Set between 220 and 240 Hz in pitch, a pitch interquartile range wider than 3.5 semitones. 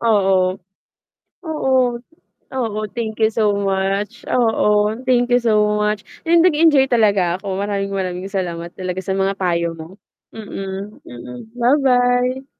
No: high, 210 Hz; average, 4.2 semitones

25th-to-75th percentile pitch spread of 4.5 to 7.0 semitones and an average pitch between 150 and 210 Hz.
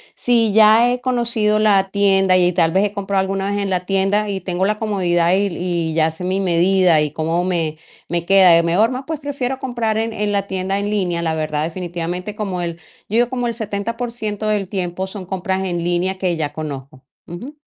No: average, 3.4 semitones; high, 190 Hz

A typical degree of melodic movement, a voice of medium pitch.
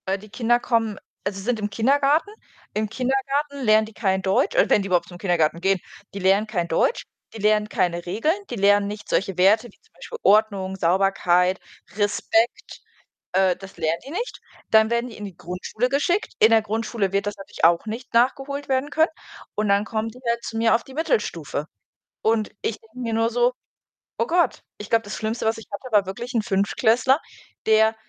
No: average, 3.6 semitones; high, 220 Hz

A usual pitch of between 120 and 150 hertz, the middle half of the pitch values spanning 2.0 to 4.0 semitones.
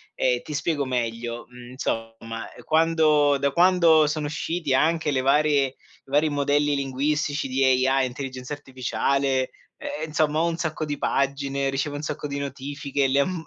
Yes: medium, 140 Hz; narrow, 2.5 semitones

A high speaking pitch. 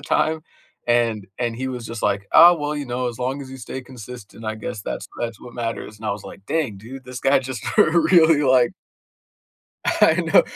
No: low, 125 Hz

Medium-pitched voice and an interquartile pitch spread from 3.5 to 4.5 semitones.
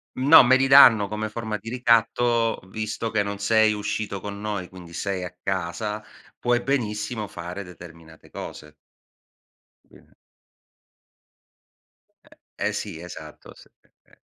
No: low, 105 Hz; average, 3.8 semitones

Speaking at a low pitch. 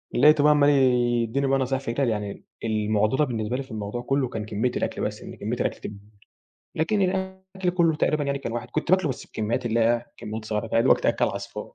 Yes: low, 125 Hz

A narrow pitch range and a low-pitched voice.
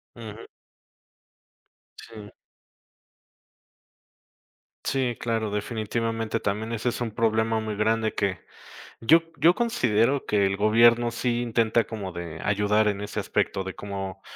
Yes: narrow, 2.3 semitones; low, 110 Hz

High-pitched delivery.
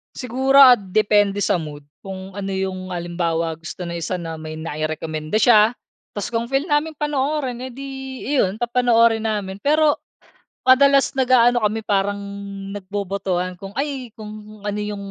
Yes: high, 210 Hz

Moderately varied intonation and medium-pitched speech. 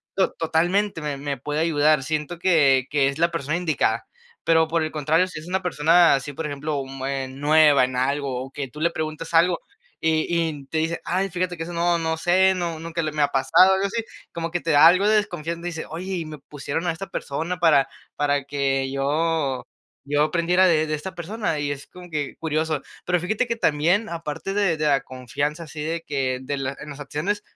Yes: average, 3.1 semitones; medium, 160 Hz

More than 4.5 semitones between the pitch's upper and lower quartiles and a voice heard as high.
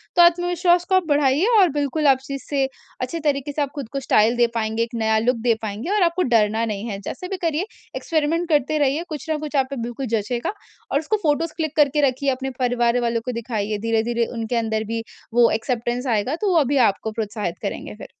Yes: average, 4.9 semitones; very high, 260 Hz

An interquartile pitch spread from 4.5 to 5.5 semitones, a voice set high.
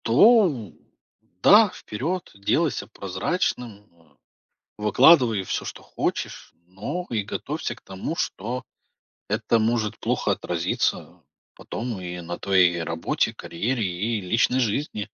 No: average, 5.0 semitones; low, 110 Hz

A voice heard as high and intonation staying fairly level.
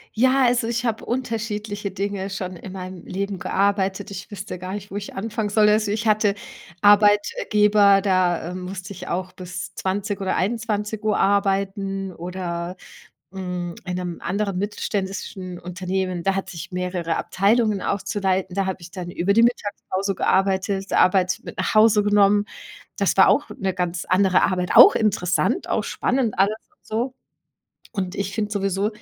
Yes: high, 195 Hz; narrow, 2.1 semitones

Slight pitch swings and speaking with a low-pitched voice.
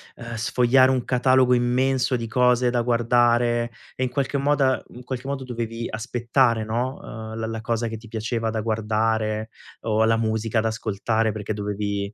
Yes: narrow, 2.1 semitones; low, 115 Hz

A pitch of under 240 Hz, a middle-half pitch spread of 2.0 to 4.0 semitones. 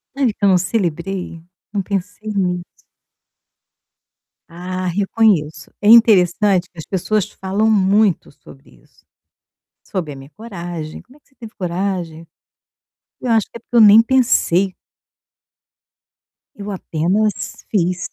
Yes: high, 190 Hz; average, 3.5 semitones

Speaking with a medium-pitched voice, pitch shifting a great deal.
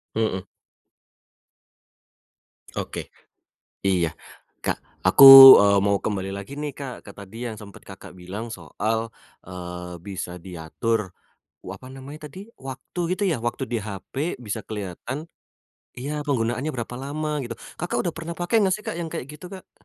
No: low, 115 Hz; wide, 6.9 semitones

